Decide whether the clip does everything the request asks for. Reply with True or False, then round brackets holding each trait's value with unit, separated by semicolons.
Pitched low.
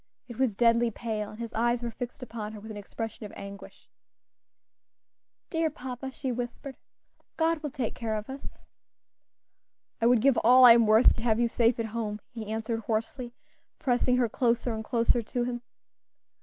False (235 Hz)